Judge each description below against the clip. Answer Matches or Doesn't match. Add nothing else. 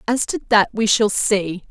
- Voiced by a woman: Matches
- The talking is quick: Matches